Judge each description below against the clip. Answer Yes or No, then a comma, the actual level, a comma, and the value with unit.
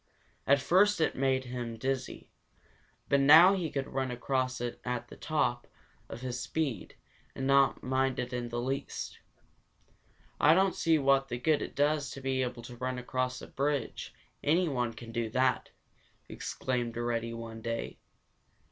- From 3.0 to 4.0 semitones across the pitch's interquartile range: No, narrow, 2.6 semitones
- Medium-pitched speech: No, low, 130 Hz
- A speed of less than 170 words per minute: Yes, average, 155 wpm